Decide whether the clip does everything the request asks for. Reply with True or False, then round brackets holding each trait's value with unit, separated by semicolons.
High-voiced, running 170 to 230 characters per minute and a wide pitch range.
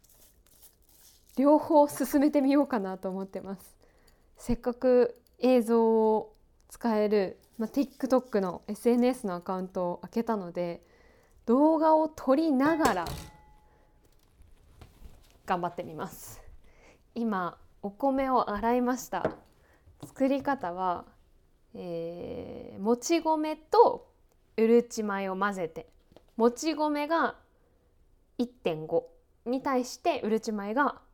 True (235 Hz; 210 characters per minute; 5.8 semitones)